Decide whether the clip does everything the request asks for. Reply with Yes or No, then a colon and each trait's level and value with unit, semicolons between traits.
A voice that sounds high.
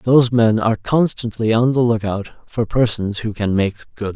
No: low, 115 Hz